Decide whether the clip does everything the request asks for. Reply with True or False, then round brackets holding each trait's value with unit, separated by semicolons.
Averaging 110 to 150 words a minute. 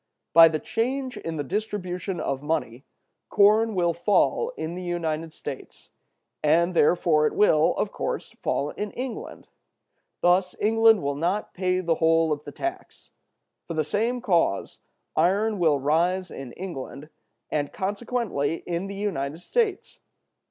True (145 wpm)